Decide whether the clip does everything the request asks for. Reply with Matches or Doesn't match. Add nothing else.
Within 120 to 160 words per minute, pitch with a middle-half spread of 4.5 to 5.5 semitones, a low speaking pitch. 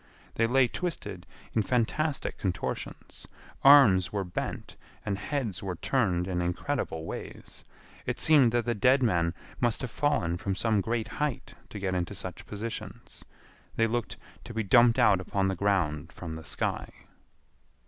Matches